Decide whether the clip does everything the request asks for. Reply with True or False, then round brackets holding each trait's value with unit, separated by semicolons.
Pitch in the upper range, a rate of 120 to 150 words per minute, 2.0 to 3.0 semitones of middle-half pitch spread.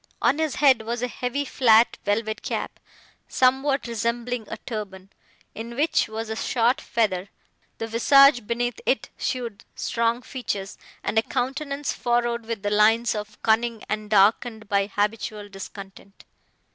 True (230 Hz; 145 wpm; 2.7 semitones)